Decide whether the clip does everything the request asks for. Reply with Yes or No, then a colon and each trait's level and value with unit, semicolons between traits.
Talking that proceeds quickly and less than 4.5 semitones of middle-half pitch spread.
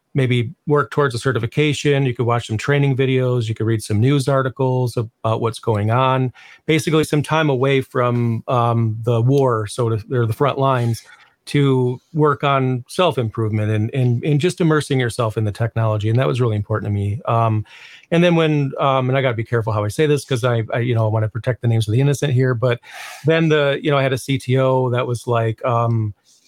Yes: fast, 220 wpm; average, 3.3 semitones